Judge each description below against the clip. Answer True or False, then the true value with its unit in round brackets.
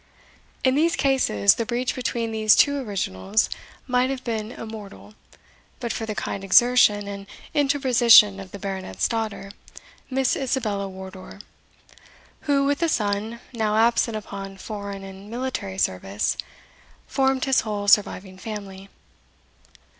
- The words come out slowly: True (130 wpm)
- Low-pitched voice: False (215 Hz)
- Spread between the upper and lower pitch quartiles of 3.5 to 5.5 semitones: True (4.1 semitones)